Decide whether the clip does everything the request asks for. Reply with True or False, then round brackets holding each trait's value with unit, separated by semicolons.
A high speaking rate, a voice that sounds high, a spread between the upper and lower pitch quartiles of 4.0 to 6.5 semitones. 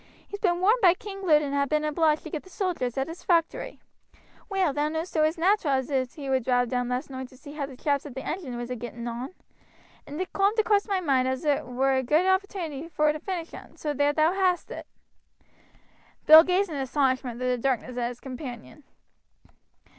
True (220 wpm; 295 Hz; 5.1 semitones)